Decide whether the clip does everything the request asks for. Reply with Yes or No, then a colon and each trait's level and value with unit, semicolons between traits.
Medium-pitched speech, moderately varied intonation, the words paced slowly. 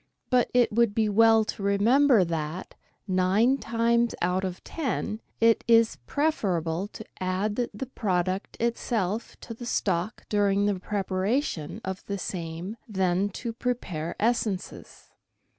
No: high, 205 Hz; average, 3.9 semitones; slow, 130 wpm